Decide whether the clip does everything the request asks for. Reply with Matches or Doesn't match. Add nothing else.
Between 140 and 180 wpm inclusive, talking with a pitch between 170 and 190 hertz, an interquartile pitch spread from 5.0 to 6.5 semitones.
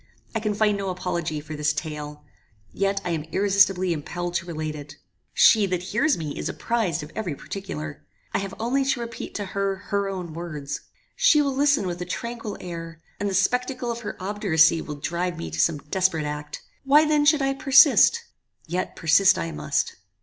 Doesn't match